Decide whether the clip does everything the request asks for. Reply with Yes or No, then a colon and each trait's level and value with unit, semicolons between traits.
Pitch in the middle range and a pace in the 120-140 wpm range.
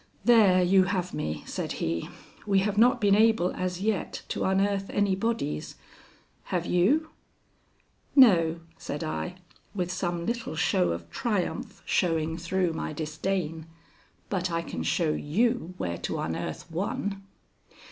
Yes: medium, 180 Hz; slow, 135 wpm